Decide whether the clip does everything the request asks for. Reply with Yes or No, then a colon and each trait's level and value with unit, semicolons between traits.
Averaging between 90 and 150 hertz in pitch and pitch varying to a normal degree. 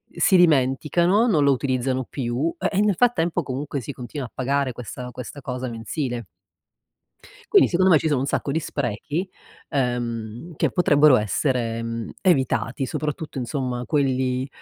Yes: low, 135 Hz; average, 3.7 semitones